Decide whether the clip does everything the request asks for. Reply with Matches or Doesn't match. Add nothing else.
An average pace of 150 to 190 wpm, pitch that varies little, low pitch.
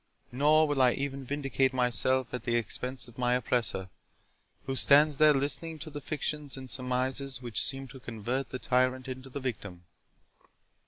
Matches